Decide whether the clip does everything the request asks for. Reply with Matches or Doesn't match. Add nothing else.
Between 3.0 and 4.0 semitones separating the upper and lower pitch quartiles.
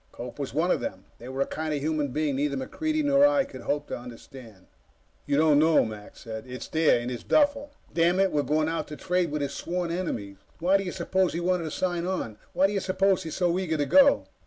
Doesn't match